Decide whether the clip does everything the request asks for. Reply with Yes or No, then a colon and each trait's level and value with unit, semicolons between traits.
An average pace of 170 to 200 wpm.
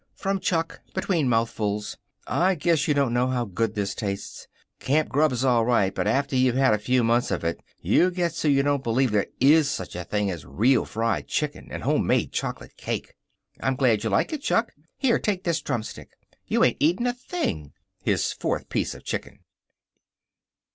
Yes: average, 190 wpm